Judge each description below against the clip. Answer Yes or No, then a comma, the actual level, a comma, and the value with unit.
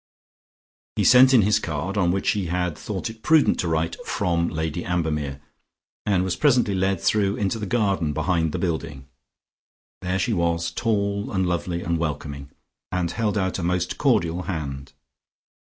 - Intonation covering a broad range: No, average, 3.5 semitones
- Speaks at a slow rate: No, average, 165 wpm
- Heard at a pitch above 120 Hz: No, very low, 90 Hz